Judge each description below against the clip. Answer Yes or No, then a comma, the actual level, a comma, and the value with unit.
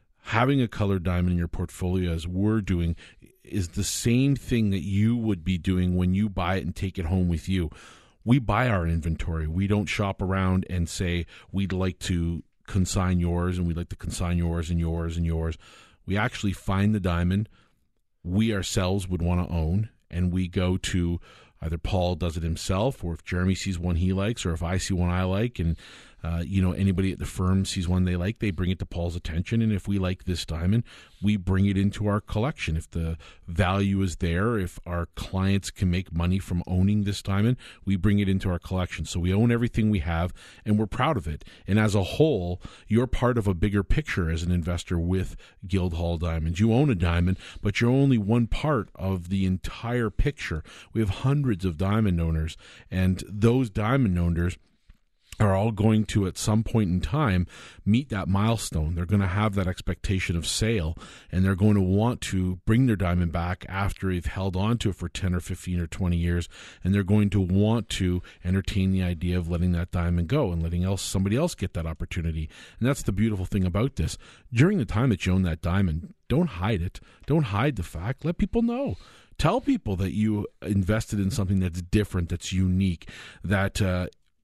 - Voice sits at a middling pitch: No, very low, 95 Hz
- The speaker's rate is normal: No, fast, 210 wpm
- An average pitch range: Yes, average, 3.1 semitones